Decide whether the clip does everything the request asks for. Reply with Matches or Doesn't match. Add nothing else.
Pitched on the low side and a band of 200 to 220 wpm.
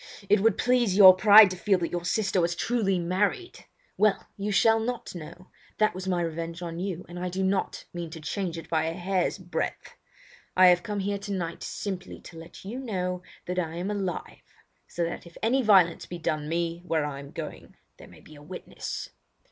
Doesn't match